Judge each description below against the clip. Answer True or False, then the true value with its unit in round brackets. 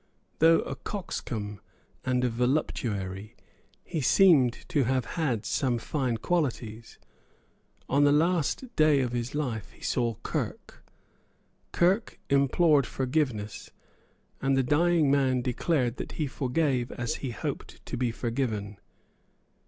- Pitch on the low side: True (130 Hz)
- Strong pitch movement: False (4.2 semitones)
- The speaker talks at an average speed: False (125 wpm)